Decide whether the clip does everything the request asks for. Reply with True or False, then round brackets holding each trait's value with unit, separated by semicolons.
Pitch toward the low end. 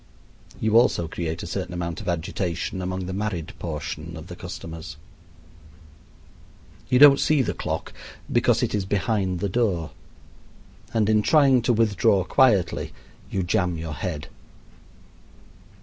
True (95 Hz)